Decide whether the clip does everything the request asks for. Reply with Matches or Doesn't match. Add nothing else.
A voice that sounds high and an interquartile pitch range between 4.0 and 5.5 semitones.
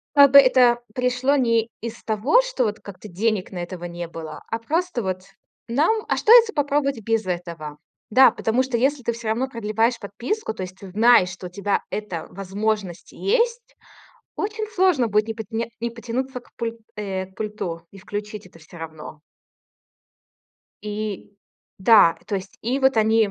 Matches